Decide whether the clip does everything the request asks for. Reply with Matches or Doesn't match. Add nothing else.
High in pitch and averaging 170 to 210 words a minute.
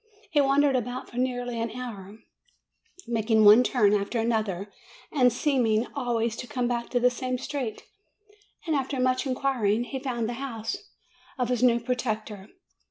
Doesn't match